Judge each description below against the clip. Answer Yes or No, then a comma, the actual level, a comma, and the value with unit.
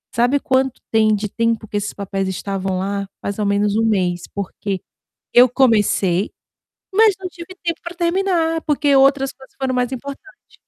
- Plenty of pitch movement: Yes, wide, 6.1 semitones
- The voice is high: Yes, high, 235 Hz